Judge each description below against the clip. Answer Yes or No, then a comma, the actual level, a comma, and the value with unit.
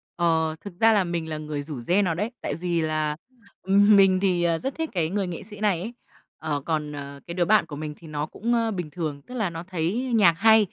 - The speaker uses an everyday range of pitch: Yes, average, 4.6 semitones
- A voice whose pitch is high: No, medium, 175 Hz